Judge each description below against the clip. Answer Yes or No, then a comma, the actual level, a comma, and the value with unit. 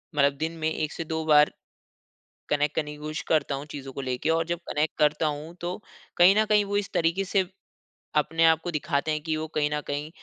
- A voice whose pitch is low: No, medium, 155 Hz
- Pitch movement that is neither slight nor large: No, narrow, 1.9 semitones